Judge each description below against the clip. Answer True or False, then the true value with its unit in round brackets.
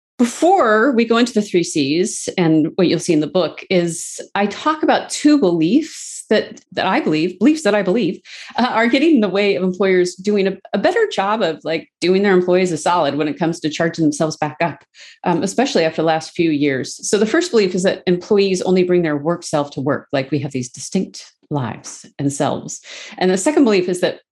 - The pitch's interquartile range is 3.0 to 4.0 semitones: False (4.7 semitones)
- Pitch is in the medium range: True (180 Hz)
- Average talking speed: False (225 wpm)